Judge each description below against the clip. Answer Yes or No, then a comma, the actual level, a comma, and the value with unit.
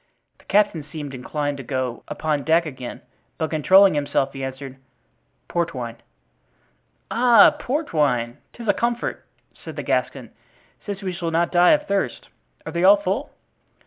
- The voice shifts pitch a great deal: Yes, wide, 6.3 semitones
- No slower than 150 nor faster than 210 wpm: Yes, average, 155 wpm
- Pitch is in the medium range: Yes, medium, 160 Hz